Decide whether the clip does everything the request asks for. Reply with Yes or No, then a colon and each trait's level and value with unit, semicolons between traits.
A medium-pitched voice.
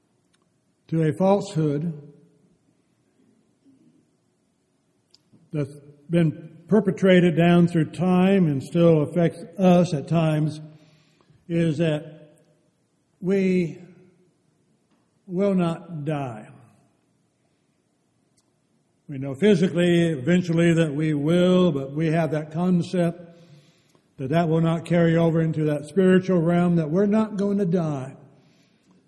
Yes: medium, 165 Hz